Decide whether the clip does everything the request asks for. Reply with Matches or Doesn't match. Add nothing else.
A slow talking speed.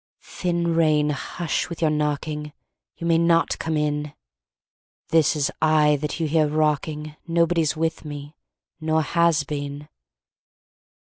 Matches